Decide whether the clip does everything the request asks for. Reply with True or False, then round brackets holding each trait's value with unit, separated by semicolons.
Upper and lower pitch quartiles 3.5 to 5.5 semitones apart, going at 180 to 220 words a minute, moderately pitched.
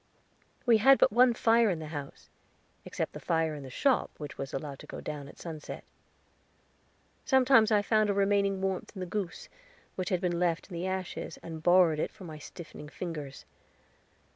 True (4.8 semitones; 190 wpm; 180 Hz)